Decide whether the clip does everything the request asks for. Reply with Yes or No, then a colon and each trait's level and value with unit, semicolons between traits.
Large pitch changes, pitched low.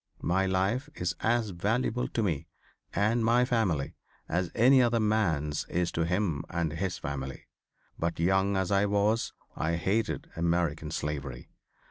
No: average, 5.0 semitones; very low, 95 Hz